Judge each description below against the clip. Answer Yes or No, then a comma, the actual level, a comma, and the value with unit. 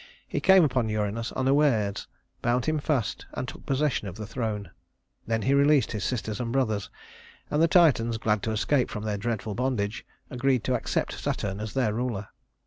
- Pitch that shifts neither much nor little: Yes, average, 4.0 semitones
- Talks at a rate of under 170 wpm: No, average, 180 wpm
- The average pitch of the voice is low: Yes, low, 115 Hz